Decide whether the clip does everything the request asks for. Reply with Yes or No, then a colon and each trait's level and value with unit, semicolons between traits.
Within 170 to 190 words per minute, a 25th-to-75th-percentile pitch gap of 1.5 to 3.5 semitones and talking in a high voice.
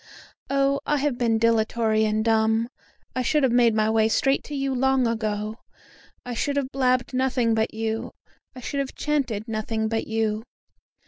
Yes: average, 175 wpm; average, 3.2 semitones; high, 230 Hz